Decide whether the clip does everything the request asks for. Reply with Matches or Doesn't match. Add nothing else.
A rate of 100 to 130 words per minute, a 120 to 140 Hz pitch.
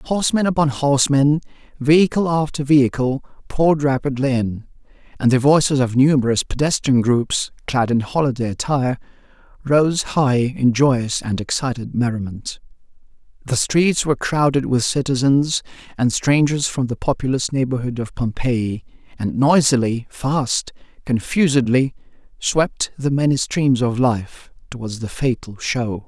Matches